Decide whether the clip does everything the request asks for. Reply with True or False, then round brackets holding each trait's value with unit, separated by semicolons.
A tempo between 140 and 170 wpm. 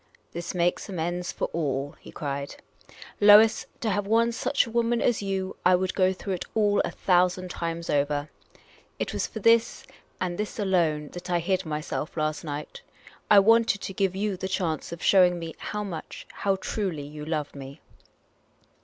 False (190 wpm)